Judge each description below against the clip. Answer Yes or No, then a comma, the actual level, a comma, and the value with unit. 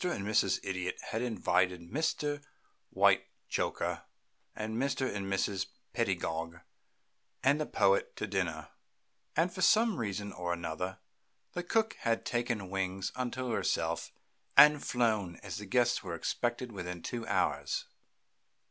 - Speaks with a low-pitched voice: Yes, low, 110 Hz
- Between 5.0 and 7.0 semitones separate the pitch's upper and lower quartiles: Yes, wide, 5.6 semitones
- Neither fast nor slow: No, slow, 130 wpm